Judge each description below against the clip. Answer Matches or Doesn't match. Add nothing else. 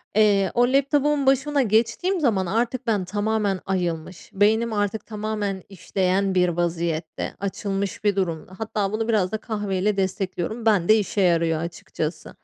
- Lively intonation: Doesn't match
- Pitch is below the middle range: Doesn't match